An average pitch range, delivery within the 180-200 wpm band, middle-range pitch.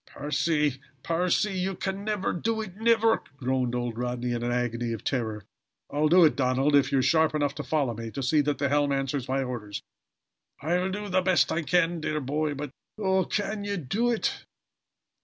No: wide, 6.3 semitones; average, 195 wpm; medium, 150 Hz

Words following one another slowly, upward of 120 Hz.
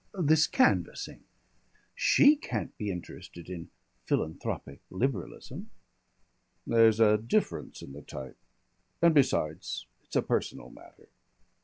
No: slow, 110 wpm; low, 110 Hz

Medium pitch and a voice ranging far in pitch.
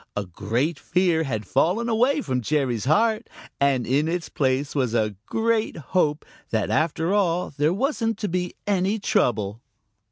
Yes: medium, 160 Hz; wide, 7.7 semitones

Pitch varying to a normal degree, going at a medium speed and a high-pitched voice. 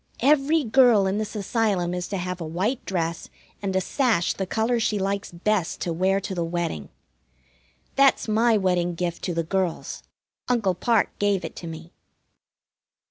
Yes: average, 4.0 semitones; average, 170 wpm; high, 195 Hz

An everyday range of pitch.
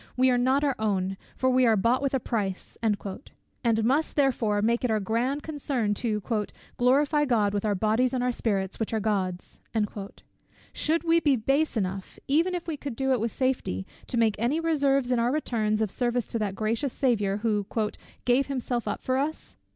Yes: average, 4.1 semitones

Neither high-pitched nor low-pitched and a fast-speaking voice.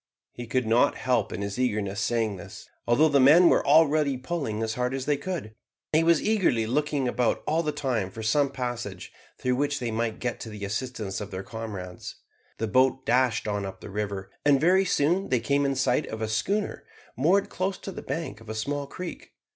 No: low, 125 Hz; fast, 210 wpm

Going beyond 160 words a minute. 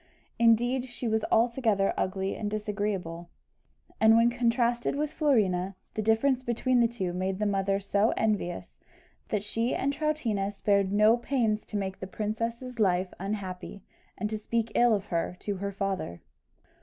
No: average, 155 wpm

